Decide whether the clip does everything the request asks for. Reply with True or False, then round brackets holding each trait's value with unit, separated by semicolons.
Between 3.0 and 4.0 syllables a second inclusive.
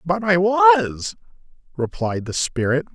True (3.7 syllables/s)